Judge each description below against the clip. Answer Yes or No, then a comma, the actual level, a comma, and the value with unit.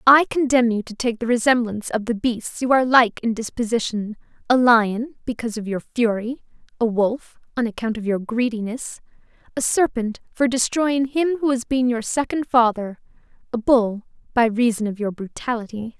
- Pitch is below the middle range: No, high, 235 Hz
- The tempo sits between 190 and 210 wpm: No, average, 160 wpm